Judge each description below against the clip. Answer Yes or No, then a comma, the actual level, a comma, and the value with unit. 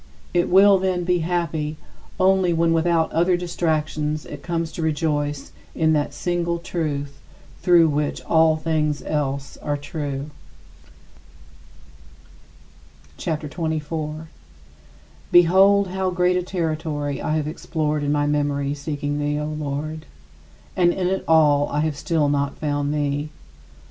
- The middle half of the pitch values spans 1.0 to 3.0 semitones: Yes, average, 2.7 semitones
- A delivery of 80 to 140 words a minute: Yes, slow, 135 wpm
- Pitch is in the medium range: Yes, medium, 155 Hz